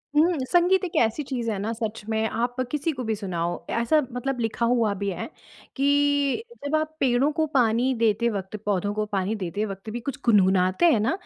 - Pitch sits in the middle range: No, high, 235 Hz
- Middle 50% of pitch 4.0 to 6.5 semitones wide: Yes, average, 5.1 semitones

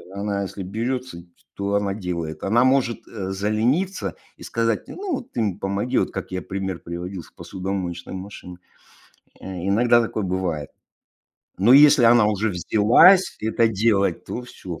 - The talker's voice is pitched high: No, low, 100 Hz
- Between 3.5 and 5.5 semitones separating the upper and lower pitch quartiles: Yes, average, 4.0 semitones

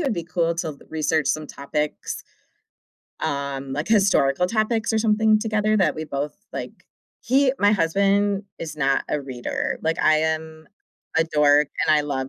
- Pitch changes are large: Yes, wide, 5.7 semitones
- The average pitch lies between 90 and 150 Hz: No, medium, 160 Hz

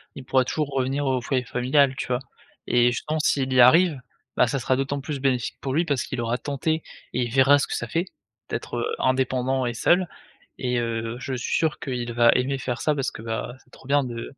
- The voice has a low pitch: Yes, low, 130 Hz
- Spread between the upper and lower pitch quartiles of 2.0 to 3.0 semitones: Yes, narrow, 2.4 semitones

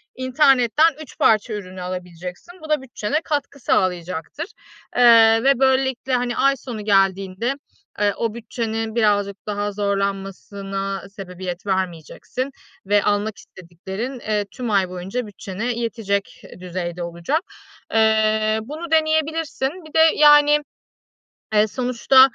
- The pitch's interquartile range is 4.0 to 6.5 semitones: Yes, average, 5.2 semitones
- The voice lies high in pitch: Yes, high, 215 Hz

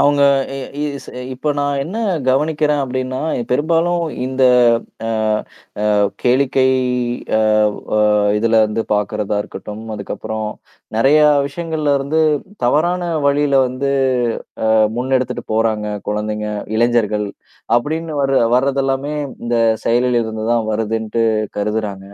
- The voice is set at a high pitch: No, low, 130 Hz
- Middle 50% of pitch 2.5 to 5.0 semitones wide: Yes, average, 4.7 semitones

